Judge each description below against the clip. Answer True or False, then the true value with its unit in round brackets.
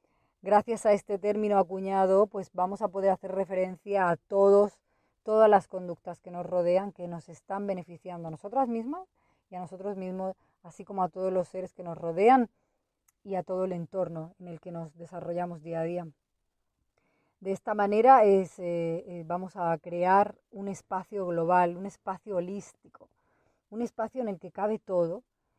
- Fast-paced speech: False (170 wpm)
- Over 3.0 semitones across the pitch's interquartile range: False (2.4 semitones)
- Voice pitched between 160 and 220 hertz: True (190 Hz)